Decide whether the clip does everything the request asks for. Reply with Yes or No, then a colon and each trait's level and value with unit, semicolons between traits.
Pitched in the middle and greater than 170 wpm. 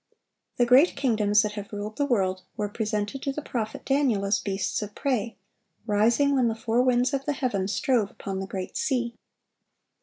No: high, 225 Hz; average, 185 wpm